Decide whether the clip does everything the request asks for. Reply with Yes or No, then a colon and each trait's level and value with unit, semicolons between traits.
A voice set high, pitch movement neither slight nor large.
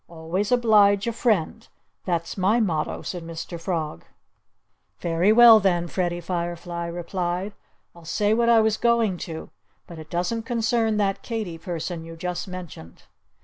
No: medium, 180 Hz; average, 4.2 semitones